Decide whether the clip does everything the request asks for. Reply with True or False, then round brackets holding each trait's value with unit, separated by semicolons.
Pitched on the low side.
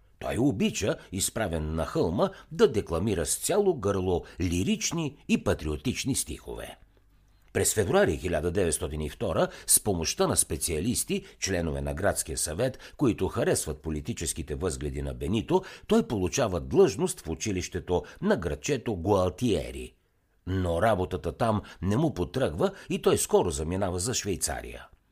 True (90 Hz)